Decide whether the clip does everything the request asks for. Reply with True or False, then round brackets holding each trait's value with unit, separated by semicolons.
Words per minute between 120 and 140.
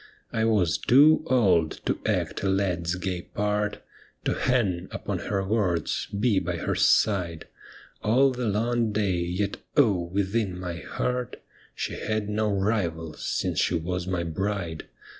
False (150 wpm)